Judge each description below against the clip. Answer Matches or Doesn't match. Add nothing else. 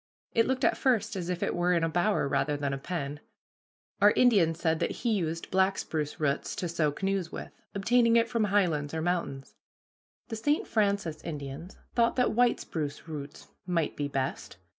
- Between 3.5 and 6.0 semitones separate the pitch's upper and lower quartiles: Matches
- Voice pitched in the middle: Matches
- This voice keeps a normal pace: Matches